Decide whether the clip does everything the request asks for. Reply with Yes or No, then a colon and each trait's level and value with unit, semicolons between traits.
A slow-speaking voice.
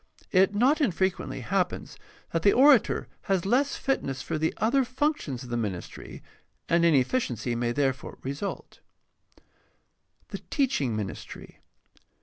Yes: slow, 130 wpm